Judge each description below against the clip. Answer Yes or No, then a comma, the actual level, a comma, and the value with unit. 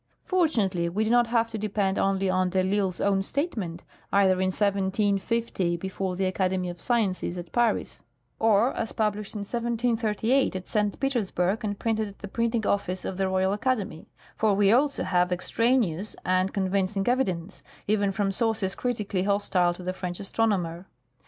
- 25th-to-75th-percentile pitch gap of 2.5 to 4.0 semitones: Yes, average, 3.1 semitones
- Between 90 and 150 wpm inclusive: No, average, 165 wpm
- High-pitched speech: Yes, high, 200 Hz